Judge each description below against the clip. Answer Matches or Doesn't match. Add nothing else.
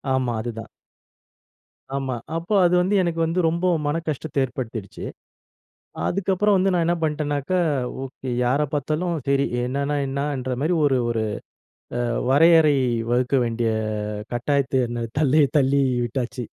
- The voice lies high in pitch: Doesn't match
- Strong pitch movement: Doesn't match